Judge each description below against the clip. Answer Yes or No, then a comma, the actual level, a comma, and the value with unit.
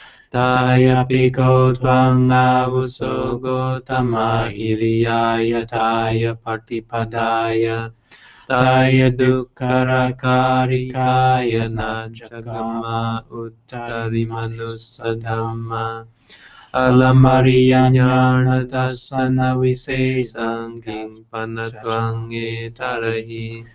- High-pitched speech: No, low, 115 Hz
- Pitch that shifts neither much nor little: No, narrow, 2.0 semitones